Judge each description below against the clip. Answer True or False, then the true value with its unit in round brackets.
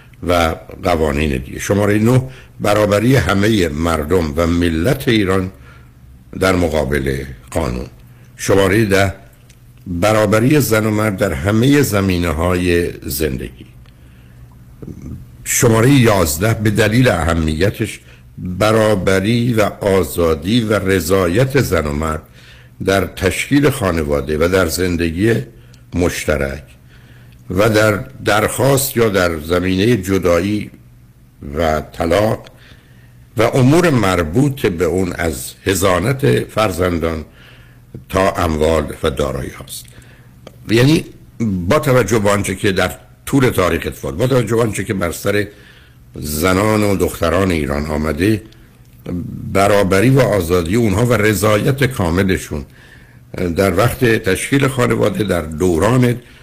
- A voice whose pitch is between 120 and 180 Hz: False (95 Hz)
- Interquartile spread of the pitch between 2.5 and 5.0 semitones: False (5.6 semitones)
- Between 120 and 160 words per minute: False (105 wpm)